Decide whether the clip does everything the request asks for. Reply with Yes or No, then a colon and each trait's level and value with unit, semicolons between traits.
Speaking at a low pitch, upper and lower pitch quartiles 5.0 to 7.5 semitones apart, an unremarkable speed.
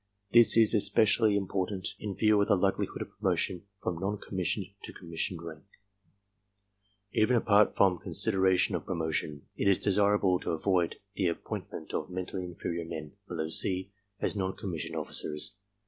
No: very low, 95 Hz; average, 3.2 semitones; average, 165 wpm